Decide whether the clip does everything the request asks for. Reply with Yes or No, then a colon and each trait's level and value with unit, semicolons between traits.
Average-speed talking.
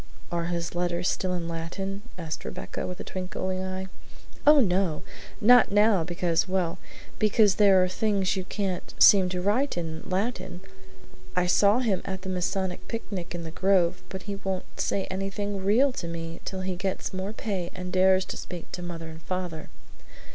Yes: average, 175 wpm